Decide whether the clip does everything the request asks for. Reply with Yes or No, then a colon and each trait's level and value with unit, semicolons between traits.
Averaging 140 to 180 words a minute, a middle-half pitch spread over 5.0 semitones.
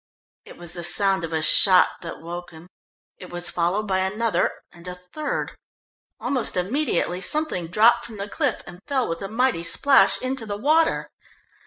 Yes: average, 175 wpm; wide, 5.5 semitones